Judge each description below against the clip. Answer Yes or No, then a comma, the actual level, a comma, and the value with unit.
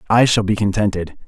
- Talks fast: No, average, 190 wpm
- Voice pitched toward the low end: Yes, low, 105 Hz